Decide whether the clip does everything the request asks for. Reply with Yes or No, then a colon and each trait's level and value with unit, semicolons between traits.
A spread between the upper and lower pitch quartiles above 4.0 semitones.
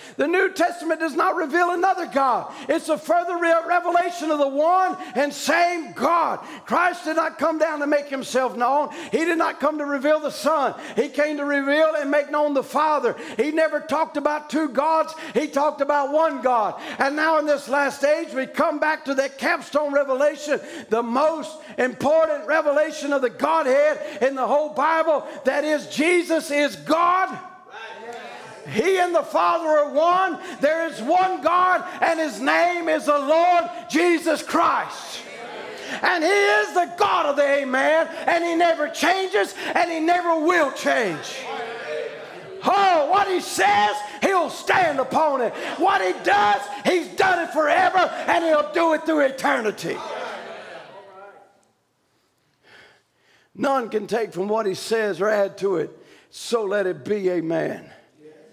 No: average, 3.5 semitones